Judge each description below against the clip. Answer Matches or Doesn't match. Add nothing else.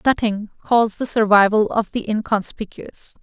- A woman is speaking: Matches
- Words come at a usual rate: Doesn't match